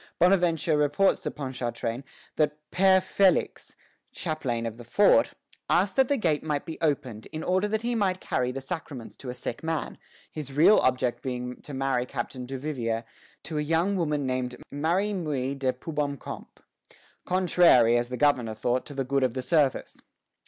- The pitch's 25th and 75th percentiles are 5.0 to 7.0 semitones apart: Yes, average, 5.3 semitones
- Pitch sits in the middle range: Yes, medium, 145 Hz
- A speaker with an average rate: Yes, average, 170 wpm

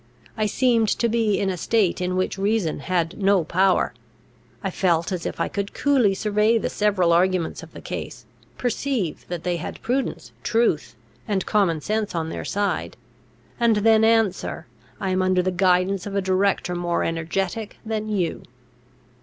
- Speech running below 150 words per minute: No, average, 170 wpm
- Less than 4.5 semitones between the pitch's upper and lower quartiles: Yes, average, 3.3 semitones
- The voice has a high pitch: Yes, high, 195 Hz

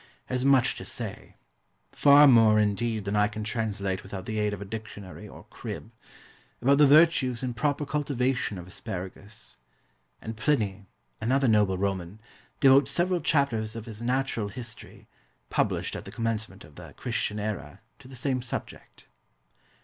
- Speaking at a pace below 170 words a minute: Yes, average, 155 wpm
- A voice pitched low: Yes, low, 110 Hz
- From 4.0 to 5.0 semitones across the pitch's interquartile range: Yes, average, 4.3 semitones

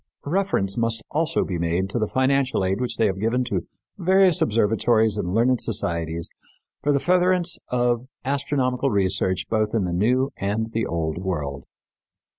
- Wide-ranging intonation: Yes, wide, 5.7 semitones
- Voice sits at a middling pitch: No, low, 115 Hz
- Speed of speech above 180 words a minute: No, average, 160 wpm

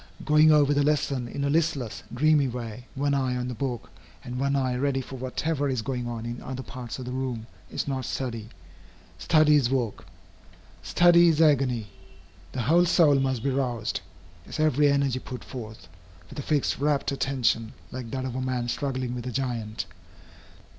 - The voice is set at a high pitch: No, low, 130 Hz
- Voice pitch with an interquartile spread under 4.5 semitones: Yes, narrow, 2.6 semitones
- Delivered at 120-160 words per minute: No, average, 180 wpm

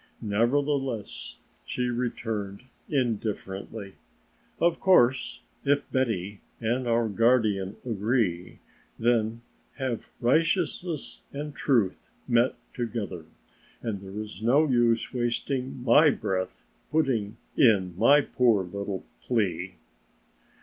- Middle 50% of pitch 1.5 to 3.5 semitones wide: No, average, 4.2 semitones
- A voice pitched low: Yes, low, 115 Hz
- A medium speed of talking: No, slow, 100 wpm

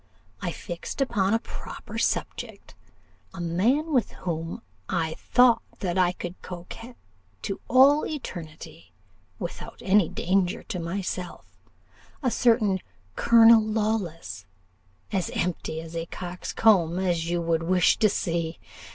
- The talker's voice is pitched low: No, medium, 185 Hz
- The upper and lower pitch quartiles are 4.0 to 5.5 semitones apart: Yes, average, 5.0 semitones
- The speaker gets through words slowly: Yes, slow, 120 wpm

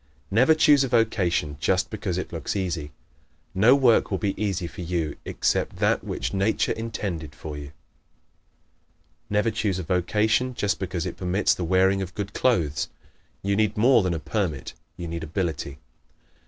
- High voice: No, very low, 95 Hz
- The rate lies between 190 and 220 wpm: No, average, 165 wpm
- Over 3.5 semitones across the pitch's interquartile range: Yes, average, 4.2 semitones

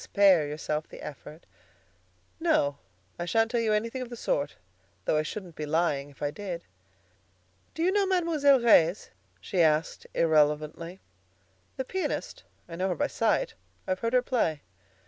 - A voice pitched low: No, medium, 180 Hz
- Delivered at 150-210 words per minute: Yes, average, 160 wpm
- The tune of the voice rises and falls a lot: Yes, wide, 7.6 semitones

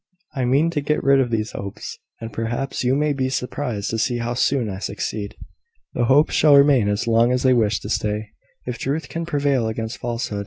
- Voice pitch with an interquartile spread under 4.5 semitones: Yes, average, 3.7 semitones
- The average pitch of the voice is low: Yes, low, 120 Hz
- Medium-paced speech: No, fast, 210 wpm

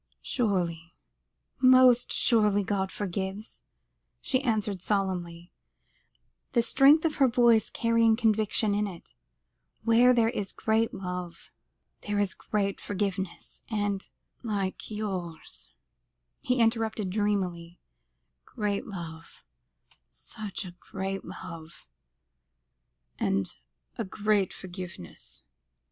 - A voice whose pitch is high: Yes, high, 205 Hz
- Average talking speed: No, slow, 100 wpm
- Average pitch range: Yes, average, 3.4 semitones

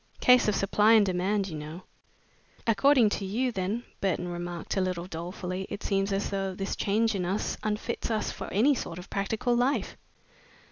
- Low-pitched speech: No, high, 195 Hz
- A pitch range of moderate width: Yes, average, 3.2 semitones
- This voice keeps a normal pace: Yes, average, 180 wpm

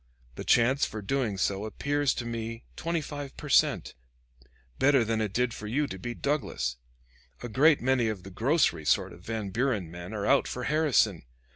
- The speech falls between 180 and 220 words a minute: Yes, average, 185 wpm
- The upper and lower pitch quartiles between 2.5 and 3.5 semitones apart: No, average, 5.1 semitones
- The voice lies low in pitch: Yes, low, 115 Hz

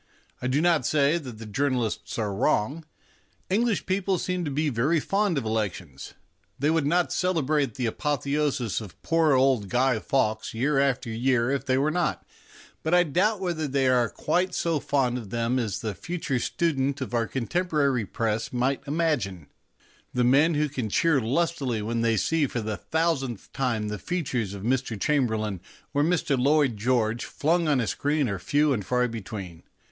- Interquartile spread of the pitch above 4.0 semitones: Yes, average, 5.2 semitones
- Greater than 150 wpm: Yes, average, 175 wpm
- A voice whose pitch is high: No, low, 135 Hz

